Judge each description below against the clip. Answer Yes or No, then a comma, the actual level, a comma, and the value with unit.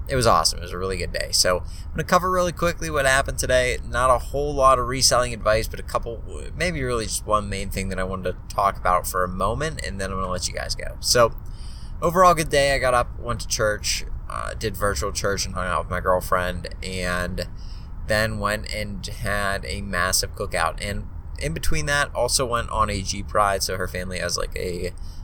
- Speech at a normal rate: No, fast, 230 wpm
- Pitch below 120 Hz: Yes, low, 100 Hz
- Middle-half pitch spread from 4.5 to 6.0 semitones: Yes, average, 4.8 semitones